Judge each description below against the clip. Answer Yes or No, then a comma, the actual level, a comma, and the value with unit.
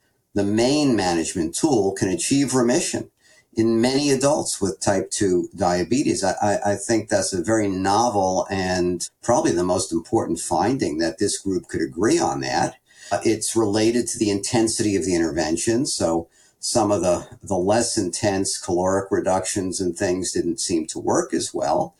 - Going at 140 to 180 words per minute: Yes, average, 160 wpm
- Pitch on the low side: Yes, low, 105 Hz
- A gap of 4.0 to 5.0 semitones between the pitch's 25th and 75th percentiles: Yes, average, 4.3 semitones